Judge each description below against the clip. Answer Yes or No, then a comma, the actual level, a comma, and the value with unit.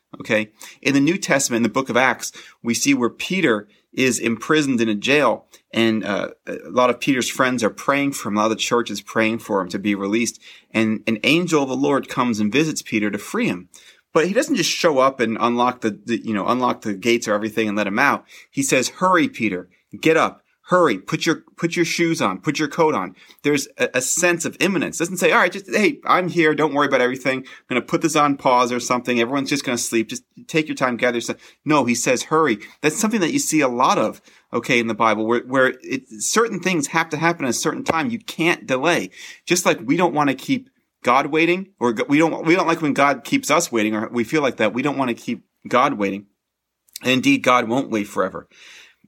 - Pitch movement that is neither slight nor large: No, wide, 6.0 semitones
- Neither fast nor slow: No, fast, 245 wpm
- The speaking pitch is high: No, low, 135 Hz